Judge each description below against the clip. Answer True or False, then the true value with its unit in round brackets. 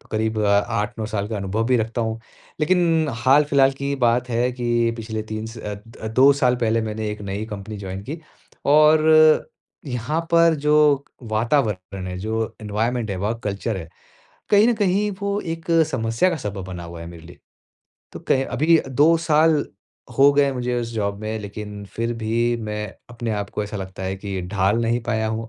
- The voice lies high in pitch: False (115 Hz)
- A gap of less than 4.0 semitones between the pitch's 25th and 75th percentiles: False (5.1 semitones)